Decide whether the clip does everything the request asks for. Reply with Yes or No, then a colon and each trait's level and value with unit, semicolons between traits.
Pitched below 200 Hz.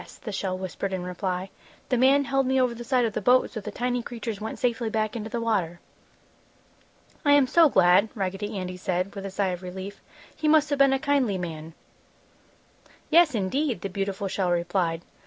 No: high, 210 Hz